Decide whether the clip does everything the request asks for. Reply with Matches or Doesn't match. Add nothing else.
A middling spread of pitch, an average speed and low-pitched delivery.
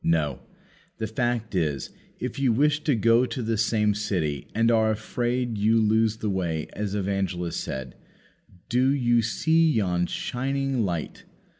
Matches